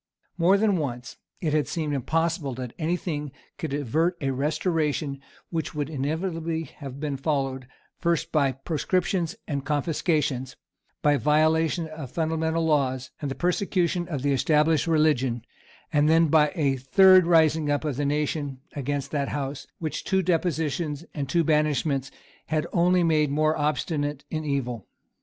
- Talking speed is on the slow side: No, average, 150 wpm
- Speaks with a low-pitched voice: No, medium, 150 Hz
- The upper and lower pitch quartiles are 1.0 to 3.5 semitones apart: Yes, average, 2.7 semitones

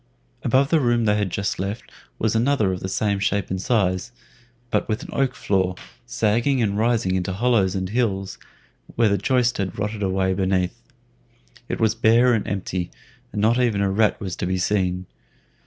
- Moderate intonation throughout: Yes, average, 3.7 semitones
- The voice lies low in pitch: Yes, low, 105 Hz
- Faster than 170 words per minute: Yes, average, 185 wpm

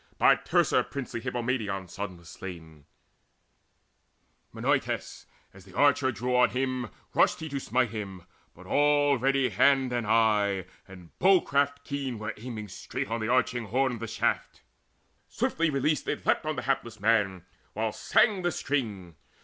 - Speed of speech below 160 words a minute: Yes, average, 150 wpm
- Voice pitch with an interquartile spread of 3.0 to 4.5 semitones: No, average, 5.1 semitones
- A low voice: Yes, low, 120 Hz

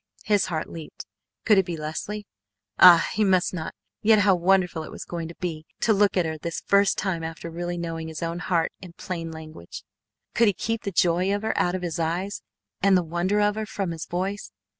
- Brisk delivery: Yes, fast, 220 wpm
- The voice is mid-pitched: Yes, medium, 175 Hz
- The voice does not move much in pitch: No, average, 3.1 semitones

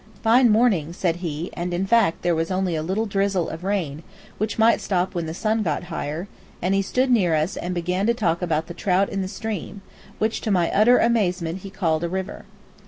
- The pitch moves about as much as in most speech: Yes, average, 3.6 semitones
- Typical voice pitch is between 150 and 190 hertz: Yes, medium, 185 Hz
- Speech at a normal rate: No, fast, 220 wpm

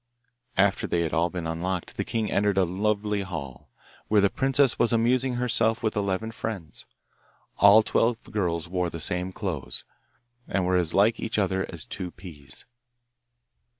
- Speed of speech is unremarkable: Yes, average, 160 wpm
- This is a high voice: No, very low, 95 Hz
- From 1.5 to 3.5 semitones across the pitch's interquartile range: No, average, 4.0 semitones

